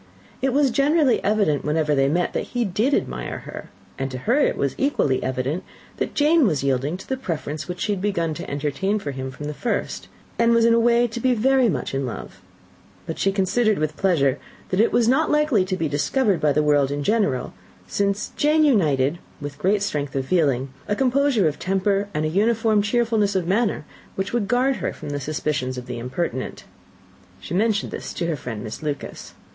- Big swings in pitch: Yes, wide, 8.1 semitones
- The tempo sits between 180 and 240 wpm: Yes, fast, 205 wpm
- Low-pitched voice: No, medium, 185 Hz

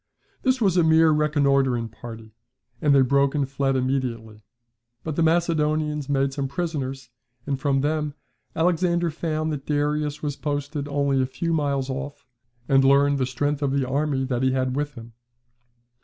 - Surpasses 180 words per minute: No, average, 165 wpm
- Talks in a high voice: No, medium, 140 Hz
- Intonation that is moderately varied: No, narrow, 2.2 semitones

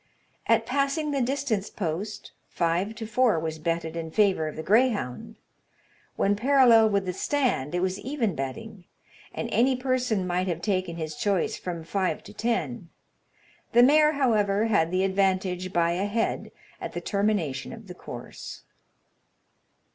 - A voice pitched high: Yes, high, 200 Hz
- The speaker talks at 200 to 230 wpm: No, average, 155 wpm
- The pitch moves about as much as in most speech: Yes, average, 5.0 semitones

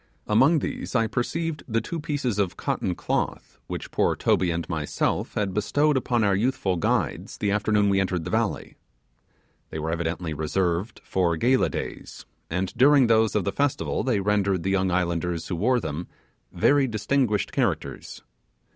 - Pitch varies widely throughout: Yes, wide, 5.9 semitones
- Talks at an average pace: Yes, average, 160 wpm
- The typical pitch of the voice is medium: No, low, 100 Hz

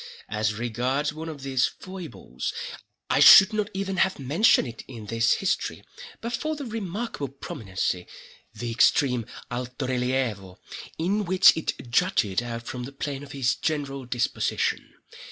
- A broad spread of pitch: Yes, wide, 7.2 semitones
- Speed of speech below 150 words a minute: Yes, slow, 135 wpm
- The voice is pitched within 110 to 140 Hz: Yes, low, 135 Hz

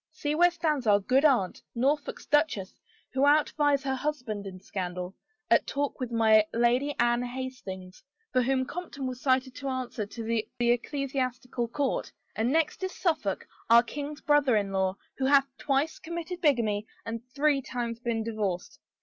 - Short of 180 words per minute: Yes, average, 160 wpm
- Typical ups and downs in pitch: Yes, average, 4.2 semitones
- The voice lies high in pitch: Yes, very high, 255 Hz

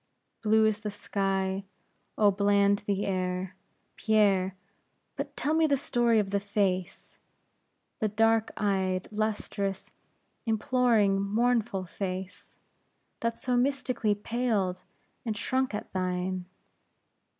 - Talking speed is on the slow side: Yes, slow, 110 wpm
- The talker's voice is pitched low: No, high, 205 Hz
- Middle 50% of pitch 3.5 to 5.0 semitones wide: No, average, 2.8 semitones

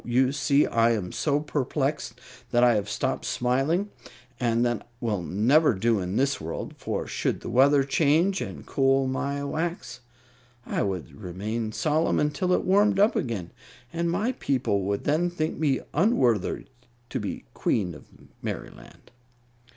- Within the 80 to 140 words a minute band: No, average, 155 wpm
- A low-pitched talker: Yes, low, 130 Hz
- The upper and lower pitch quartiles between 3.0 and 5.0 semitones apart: No, wide, 5.5 semitones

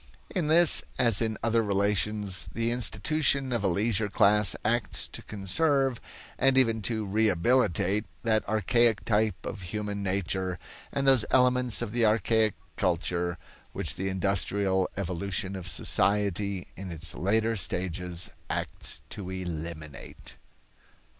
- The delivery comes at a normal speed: No, slow, 125 wpm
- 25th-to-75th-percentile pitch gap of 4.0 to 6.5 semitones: No, average, 3.6 semitones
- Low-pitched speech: Yes, low, 105 Hz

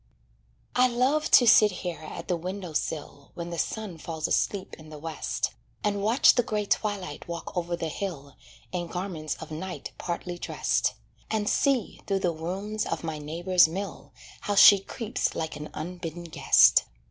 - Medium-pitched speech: Yes, medium, 180 Hz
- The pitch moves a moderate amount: Yes, average, 4.1 semitones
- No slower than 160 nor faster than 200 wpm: Yes, average, 170 wpm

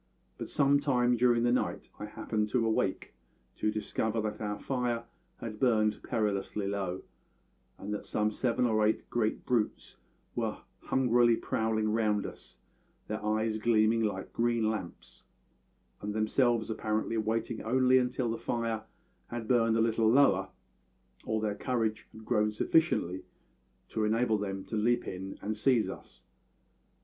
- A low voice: Yes, low, 110 Hz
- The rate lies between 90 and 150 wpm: Yes, average, 145 wpm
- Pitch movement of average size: No, narrow, 1.9 semitones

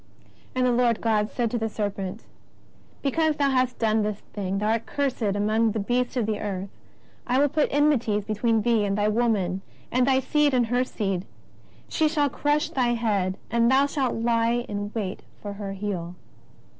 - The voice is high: Yes, high, 230 Hz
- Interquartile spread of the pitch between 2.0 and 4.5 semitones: Yes, average, 3.6 semitones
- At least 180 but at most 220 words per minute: Yes, average, 185 wpm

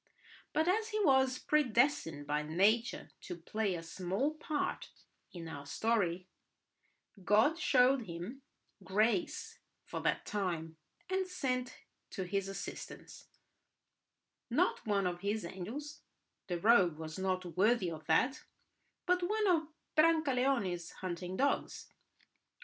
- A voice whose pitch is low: No, high, 210 Hz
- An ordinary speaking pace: No, slow, 115 wpm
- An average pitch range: No, wide, 7.6 semitones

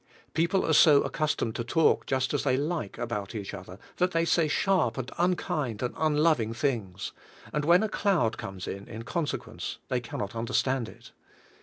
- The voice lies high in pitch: No, low, 130 Hz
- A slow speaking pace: No, average, 170 wpm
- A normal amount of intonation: No, wide, 6.2 semitones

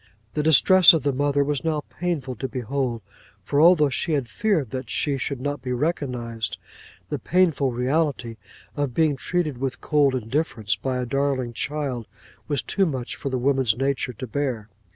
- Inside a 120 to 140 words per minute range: No, average, 170 wpm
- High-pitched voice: No, medium, 140 Hz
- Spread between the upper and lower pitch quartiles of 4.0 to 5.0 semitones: No, average, 3.1 semitones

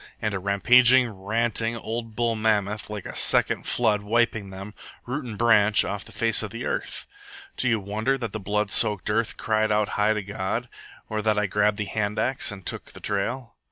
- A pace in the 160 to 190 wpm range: No, average, 200 wpm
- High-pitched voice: No, low, 110 Hz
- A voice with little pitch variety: Yes, narrow, 2.1 semitones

